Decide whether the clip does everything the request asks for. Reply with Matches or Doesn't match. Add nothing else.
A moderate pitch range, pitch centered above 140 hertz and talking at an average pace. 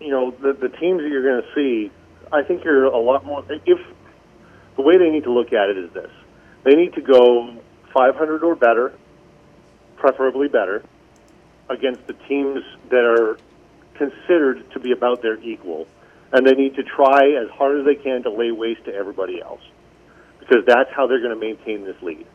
Doesn't match